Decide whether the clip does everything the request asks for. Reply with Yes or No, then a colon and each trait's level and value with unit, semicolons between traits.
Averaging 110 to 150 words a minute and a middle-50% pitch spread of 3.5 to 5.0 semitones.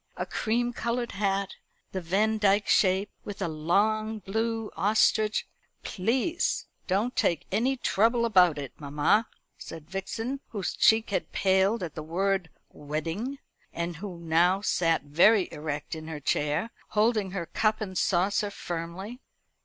Yes: average, 140 wpm; average, 4.4 semitones